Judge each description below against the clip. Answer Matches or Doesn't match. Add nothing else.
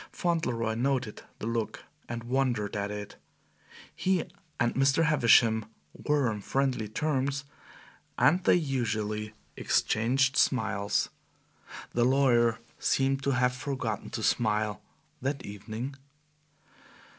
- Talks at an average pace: Doesn't match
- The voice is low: Matches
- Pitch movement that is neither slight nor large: Matches